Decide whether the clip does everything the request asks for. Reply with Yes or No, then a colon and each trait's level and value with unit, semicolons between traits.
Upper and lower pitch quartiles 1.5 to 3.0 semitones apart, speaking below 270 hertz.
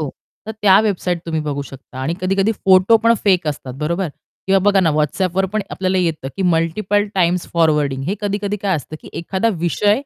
No: average, 3.8 semitones; medium, 185 Hz